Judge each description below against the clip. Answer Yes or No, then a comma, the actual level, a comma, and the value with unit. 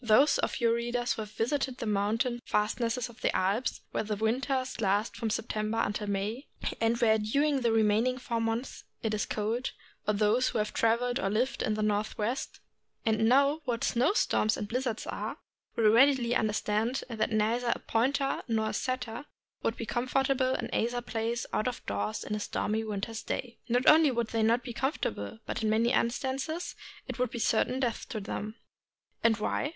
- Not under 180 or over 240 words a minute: Yes, average, 190 wpm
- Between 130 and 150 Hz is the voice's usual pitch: No, high, 230 Hz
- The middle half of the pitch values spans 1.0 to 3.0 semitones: Yes, average, 2.7 semitones